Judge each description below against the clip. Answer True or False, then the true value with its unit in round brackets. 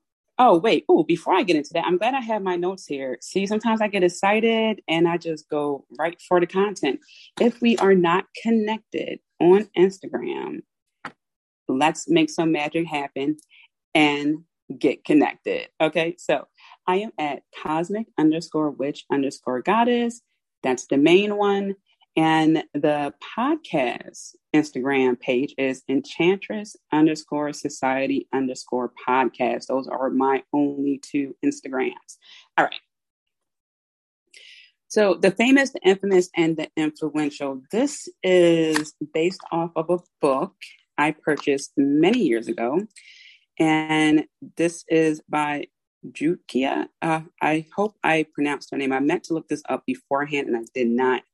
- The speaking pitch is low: False (165 Hz)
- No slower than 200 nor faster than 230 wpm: False (140 wpm)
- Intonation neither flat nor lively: False (6.9 semitones)